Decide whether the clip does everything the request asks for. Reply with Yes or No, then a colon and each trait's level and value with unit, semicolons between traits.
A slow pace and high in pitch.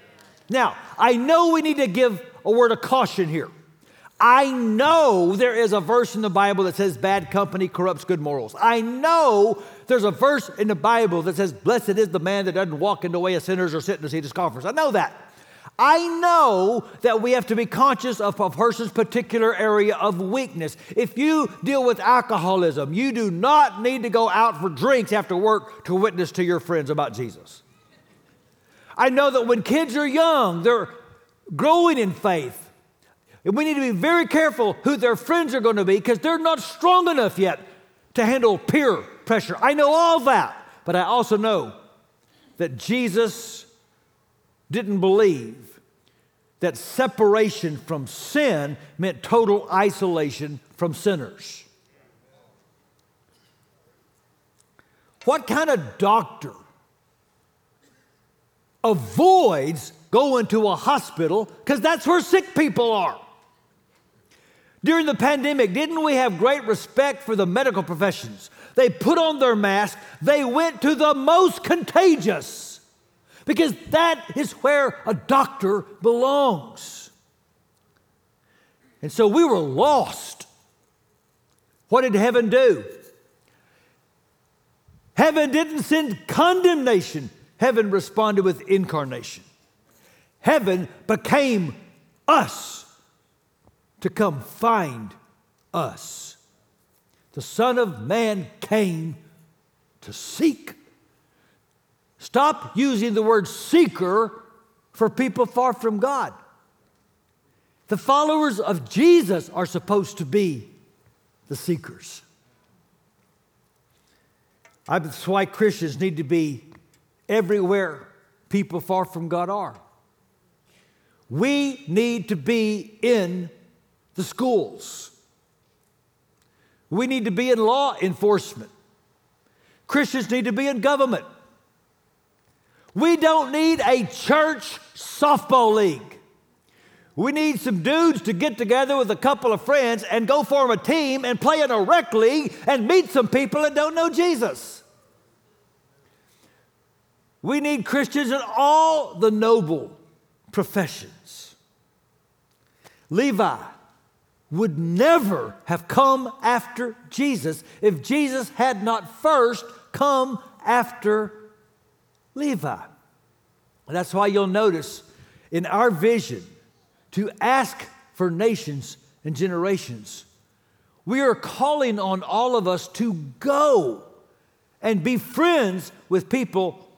Yes: slow, 125 wpm; high, 225 Hz